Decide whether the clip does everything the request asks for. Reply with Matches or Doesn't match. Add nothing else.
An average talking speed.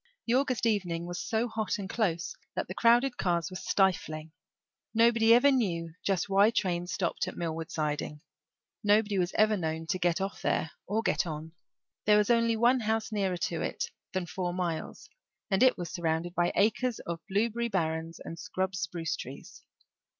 Matches